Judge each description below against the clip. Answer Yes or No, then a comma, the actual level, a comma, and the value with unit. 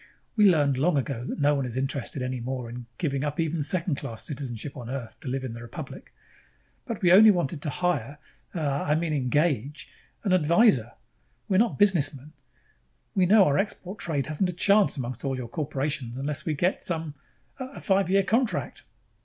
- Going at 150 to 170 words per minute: No, average, 190 wpm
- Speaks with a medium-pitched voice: Yes, medium, 150 Hz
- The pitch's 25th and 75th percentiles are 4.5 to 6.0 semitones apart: Yes, average, 5.1 semitones